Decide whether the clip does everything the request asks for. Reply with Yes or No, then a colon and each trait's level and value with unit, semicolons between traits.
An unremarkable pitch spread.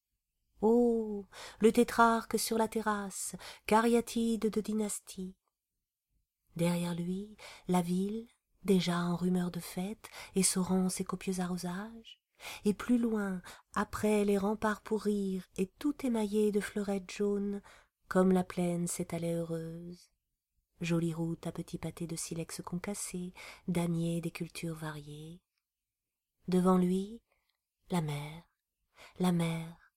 Yes: average, 3.5 semitones